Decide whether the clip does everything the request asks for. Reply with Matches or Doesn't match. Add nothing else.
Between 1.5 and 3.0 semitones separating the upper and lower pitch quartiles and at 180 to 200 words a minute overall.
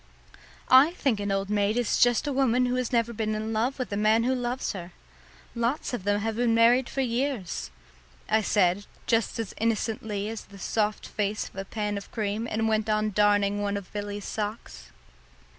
Matches